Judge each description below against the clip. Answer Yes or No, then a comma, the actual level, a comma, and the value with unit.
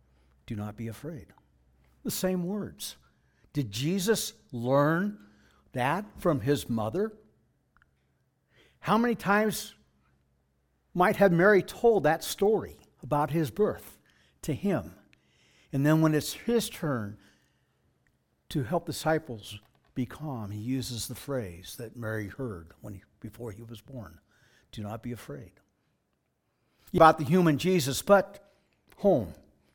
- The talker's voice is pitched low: Yes, low, 125 Hz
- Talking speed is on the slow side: Yes, slow, 125 wpm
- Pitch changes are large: Yes, wide, 8.6 semitones